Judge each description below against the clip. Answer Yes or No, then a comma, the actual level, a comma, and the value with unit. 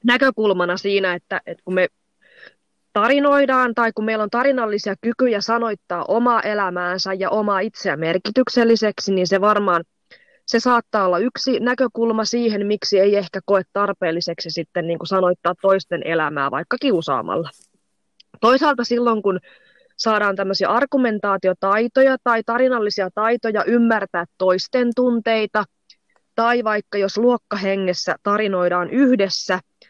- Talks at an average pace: Yes, average, 120 wpm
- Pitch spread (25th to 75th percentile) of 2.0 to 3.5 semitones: No, average, 4.0 semitones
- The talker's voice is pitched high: Yes, high, 210 Hz